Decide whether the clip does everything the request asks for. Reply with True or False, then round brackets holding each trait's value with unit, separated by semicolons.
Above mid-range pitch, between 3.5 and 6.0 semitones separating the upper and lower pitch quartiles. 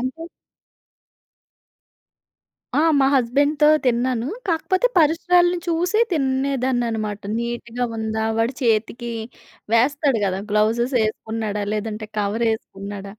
True (240 Hz; 4.2 semitones)